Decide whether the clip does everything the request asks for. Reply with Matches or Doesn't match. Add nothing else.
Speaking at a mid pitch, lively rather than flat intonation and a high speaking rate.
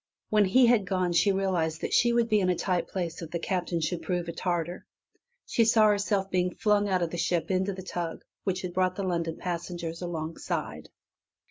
Doesn't match